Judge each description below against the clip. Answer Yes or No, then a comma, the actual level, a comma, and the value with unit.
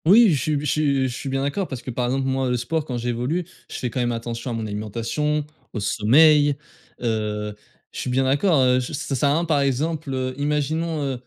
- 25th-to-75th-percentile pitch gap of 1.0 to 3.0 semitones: No, average, 3.7 semitones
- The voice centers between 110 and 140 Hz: Yes, low, 135 Hz